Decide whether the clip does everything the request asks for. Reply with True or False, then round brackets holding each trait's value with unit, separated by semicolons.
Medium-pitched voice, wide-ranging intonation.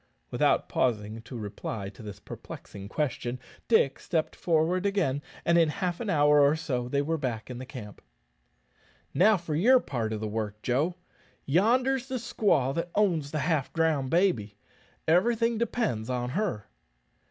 True (150 Hz; 6.9 semitones)